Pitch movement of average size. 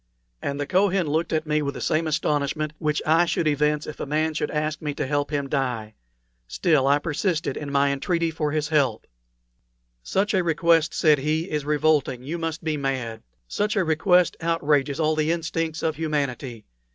No: narrow, 2.3 semitones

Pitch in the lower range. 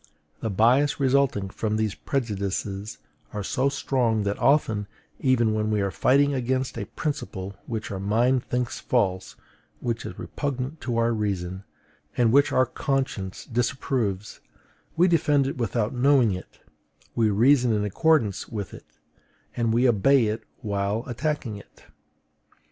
Yes: low, 115 Hz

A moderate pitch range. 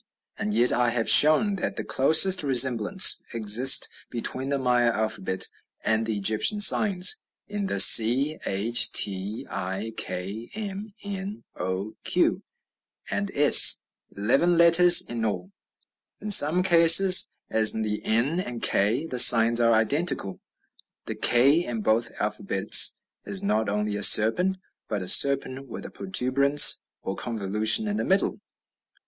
No: wide, 7.6 semitones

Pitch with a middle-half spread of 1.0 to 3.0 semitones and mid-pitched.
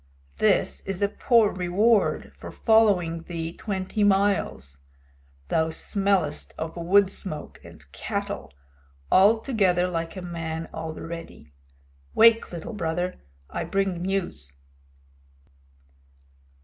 No: average, 3.5 semitones; medium, 180 Hz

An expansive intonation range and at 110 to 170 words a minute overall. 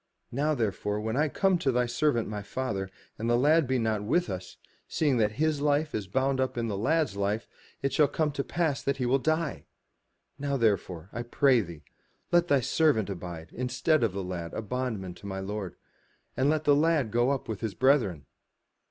No: wide, 5.8 semitones; fast, 205 wpm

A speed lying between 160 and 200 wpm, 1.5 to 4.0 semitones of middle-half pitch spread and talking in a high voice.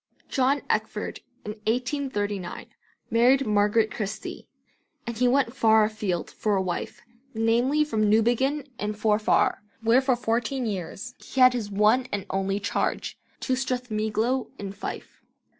No: slow, 135 wpm; average, 3.3 semitones; high, 225 Hz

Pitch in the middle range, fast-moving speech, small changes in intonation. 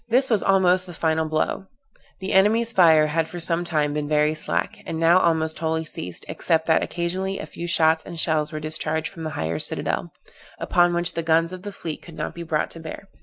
Yes: medium, 165 Hz; fast, 220 wpm; narrow, 2.2 semitones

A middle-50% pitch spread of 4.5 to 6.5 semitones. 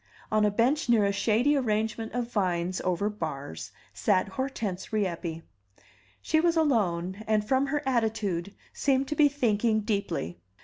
Yes: wide, 5.4 semitones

